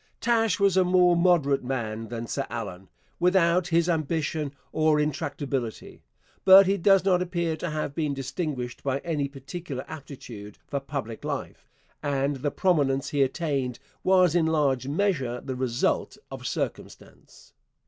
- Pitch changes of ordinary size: Yes, average, 4.7 semitones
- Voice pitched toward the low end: No, medium, 150 Hz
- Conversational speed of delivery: Yes, average, 145 wpm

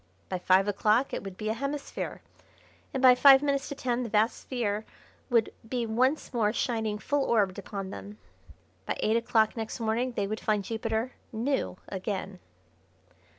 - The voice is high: Yes, high, 225 Hz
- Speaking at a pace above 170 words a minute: No, average, 165 wpm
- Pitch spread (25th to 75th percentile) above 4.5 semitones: No, average, 3.4 semitones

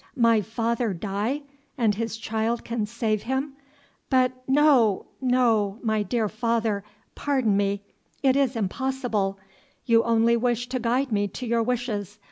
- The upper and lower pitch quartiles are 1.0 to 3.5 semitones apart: Yes, average, 2.8 semitones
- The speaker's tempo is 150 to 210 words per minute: No, average, 140 wpm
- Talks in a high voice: Yes, high, 230 Hz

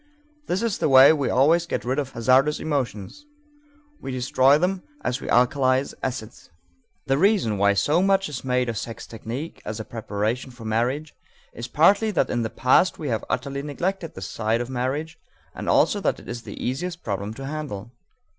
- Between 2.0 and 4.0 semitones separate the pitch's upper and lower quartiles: No, average, 4.8 semitones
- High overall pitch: No, low, 130 Hz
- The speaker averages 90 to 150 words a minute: No, average, 185 wpm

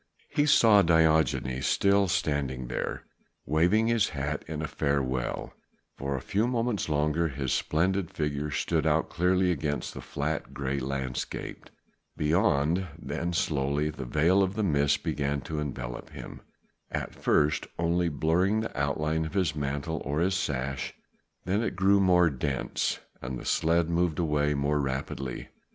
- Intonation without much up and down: No, average, 4.0 semitones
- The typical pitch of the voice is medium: No, very low, 75 Hz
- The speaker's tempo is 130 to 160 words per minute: Yes, average, 145 wpm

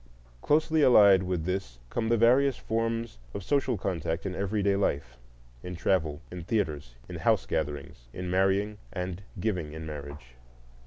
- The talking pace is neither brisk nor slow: Yes, average, 150 wpm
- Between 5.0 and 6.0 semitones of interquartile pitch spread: Yes, wide, 5.5 semitones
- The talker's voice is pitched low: Yes, very low, 95 Hz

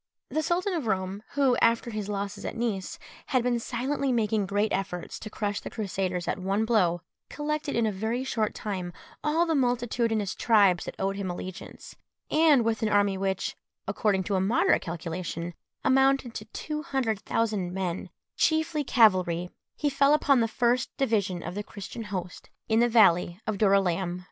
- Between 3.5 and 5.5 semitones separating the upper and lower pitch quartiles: Yes, average, 4.6 semitones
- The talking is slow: No, average, 175 wpm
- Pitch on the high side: Yes, high, 215 Hz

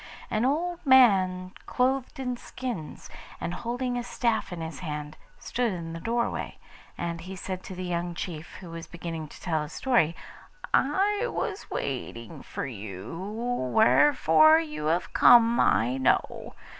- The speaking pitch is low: No, medium, 180 Hz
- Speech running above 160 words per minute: No, average, 150 wpm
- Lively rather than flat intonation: Yes, wide, 7.4 semitones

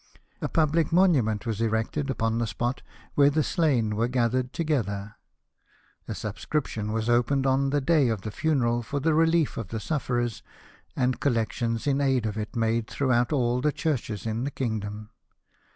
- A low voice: Yes, low, 120 Hz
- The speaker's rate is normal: Yes, average, 170 wpm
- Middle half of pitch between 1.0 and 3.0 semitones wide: No, average, 4.2 semitones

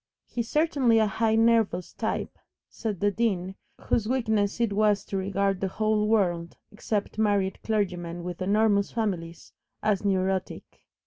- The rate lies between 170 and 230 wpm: No, average, 140 wpm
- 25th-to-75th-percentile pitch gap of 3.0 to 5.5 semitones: No, narrow, 2.6 semitones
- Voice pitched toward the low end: No, high, 205 Hz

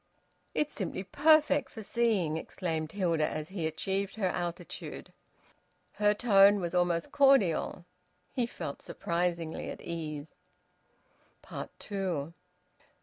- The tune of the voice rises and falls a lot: No, average, 4.1 semitones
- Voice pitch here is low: No, medium, 185 Hz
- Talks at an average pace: No, slow, 105 wpm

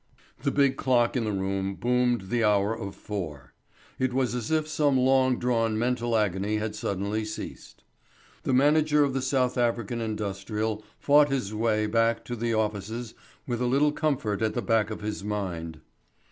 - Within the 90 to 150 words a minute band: No, average, 175 wpm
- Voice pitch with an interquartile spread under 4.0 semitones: Yes, average, 3.3 semitones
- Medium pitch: No, low, 115 Hz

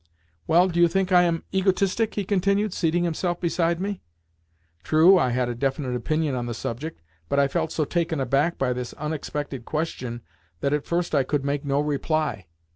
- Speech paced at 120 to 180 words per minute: No, average, 190 wpm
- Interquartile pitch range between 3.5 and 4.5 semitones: Yes, average, 4.2 semitones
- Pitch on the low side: No, medium, 155 Hz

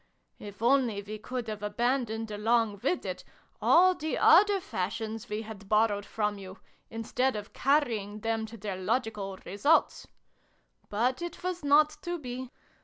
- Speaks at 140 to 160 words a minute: Yes, average, 155 wpm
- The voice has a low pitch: No, high, 225 Hz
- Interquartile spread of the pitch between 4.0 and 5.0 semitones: Yes, average, 4.3 semitones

